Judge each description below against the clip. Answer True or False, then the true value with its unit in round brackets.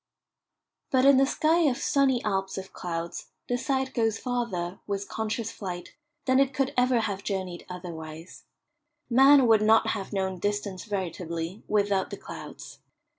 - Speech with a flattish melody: False (5.1 semitones)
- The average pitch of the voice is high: True (210 Hz)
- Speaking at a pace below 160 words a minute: True (150 wpm)